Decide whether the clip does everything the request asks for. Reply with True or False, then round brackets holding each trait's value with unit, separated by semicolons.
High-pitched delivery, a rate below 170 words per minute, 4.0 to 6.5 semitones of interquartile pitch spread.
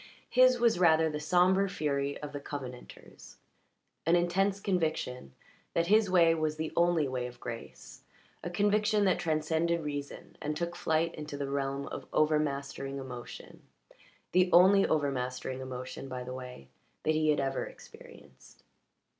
False (155 Hz; 145 wpm; 4.3 semitones)